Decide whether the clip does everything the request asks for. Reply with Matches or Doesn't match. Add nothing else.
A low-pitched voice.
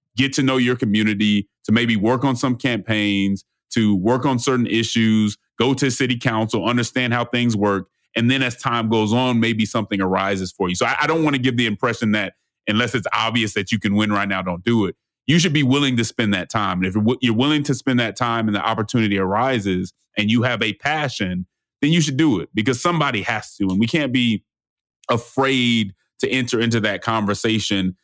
Matches